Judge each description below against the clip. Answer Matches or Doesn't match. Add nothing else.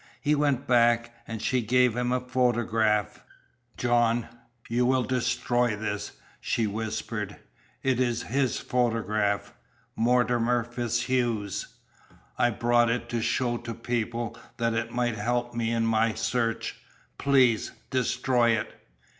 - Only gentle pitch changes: Matches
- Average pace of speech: Doesn't match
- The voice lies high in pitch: Doesn't match